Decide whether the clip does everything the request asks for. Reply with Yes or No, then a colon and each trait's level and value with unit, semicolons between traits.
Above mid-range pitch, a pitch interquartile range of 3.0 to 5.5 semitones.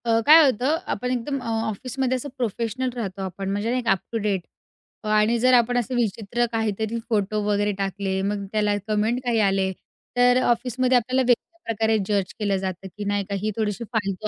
Yes: high, 220 Hz; average, 3.3 semitones